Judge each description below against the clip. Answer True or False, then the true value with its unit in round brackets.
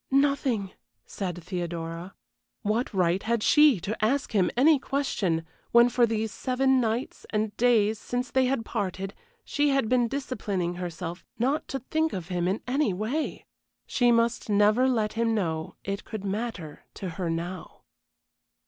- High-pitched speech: True (220 Hz)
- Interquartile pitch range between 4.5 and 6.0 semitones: True (5.3 semitones)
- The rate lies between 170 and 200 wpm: False (155 wpm)